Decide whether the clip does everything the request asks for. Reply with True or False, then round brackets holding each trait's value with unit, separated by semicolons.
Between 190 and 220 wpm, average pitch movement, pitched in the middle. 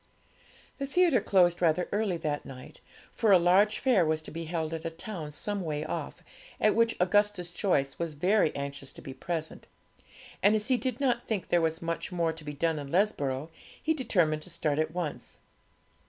True (195 wpm; 4.9 semitones; 170 Hz)